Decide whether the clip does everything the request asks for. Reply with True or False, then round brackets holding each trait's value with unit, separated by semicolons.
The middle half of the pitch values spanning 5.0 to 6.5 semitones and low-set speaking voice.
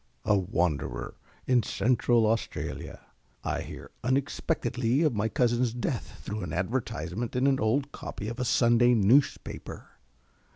False (3.2 semitones; 120 Hz)